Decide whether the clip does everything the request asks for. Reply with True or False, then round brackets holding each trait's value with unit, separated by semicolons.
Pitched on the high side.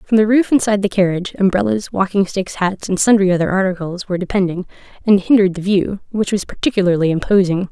True (195 Hz)